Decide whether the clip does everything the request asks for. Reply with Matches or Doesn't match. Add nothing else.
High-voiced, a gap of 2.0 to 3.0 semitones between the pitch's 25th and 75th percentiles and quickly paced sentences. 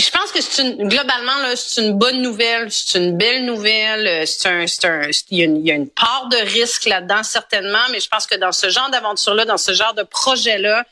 Doesn't match